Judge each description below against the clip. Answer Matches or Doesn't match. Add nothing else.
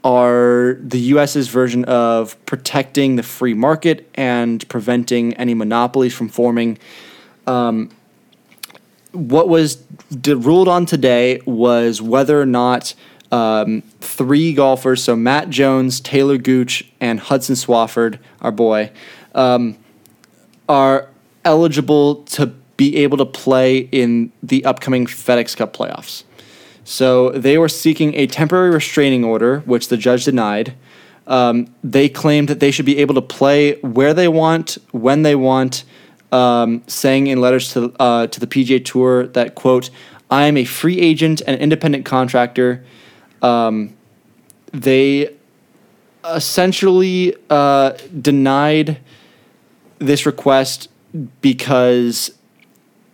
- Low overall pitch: Matches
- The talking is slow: Matches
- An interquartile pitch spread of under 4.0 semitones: Matches